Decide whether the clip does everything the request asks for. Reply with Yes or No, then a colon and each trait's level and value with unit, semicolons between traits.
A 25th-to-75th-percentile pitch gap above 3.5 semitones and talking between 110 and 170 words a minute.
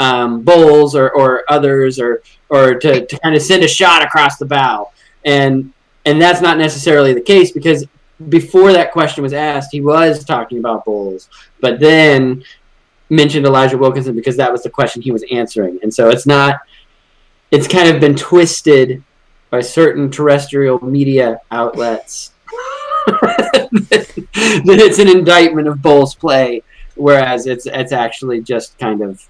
Yes: average, 4.0 semitones; average, 155 wpm